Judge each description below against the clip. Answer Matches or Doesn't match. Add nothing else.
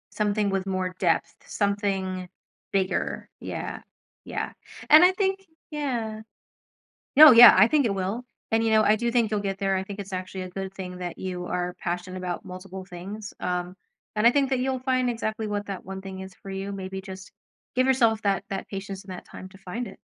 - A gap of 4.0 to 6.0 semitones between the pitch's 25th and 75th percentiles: Doesn't match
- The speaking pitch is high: Matches